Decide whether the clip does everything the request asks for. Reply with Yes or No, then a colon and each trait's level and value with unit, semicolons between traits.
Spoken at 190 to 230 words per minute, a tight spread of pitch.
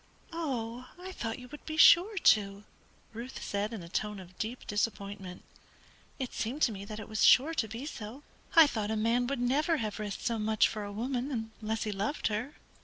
No: fast, 205 wpm; average, 4.0 semitones